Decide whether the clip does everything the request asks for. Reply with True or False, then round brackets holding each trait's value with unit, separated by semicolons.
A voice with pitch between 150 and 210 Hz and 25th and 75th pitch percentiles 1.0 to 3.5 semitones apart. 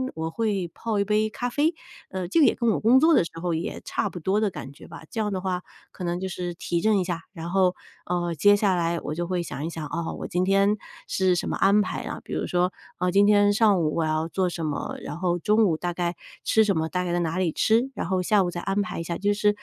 True (185 Hz; 3.2 semitones)